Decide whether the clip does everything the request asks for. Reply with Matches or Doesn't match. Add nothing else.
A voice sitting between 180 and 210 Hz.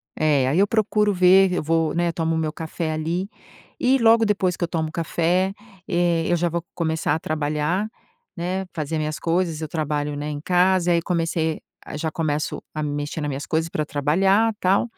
Doesn't match